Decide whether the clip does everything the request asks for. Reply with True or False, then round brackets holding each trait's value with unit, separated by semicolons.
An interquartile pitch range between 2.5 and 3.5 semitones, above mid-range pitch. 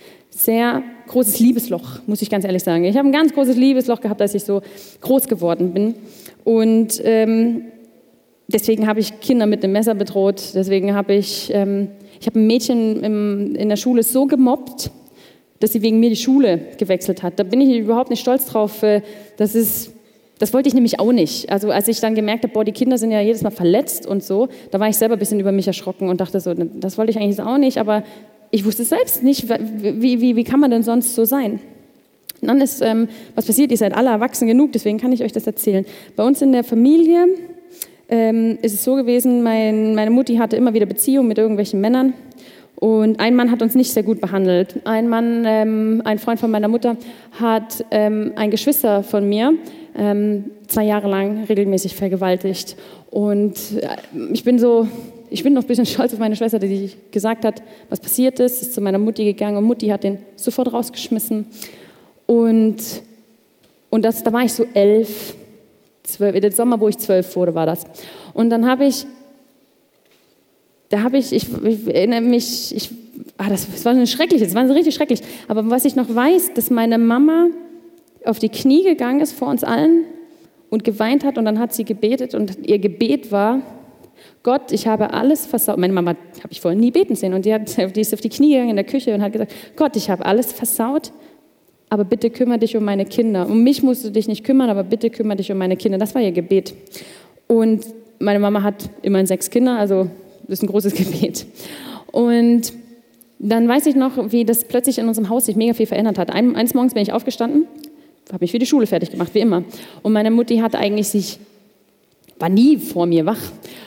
True (3.0 semitones; 225 Hz)